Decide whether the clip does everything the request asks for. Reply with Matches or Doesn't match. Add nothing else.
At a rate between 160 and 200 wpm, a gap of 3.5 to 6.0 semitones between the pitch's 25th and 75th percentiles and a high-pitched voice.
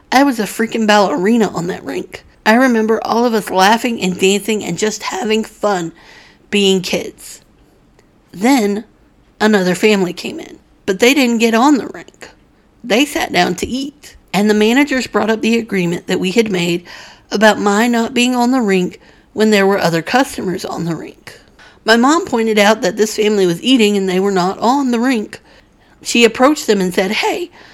Matches